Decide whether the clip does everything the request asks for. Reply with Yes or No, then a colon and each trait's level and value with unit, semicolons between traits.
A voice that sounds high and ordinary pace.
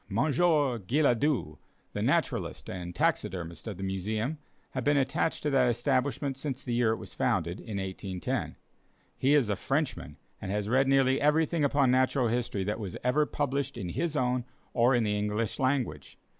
No: low, 125 Hz; average, 170 wpm